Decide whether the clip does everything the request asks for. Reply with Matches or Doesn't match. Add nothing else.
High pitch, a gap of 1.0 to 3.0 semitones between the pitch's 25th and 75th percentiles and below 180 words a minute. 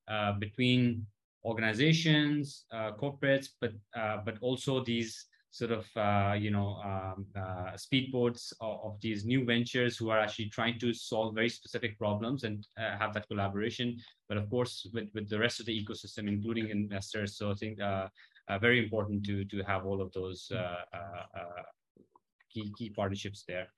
Doesn't match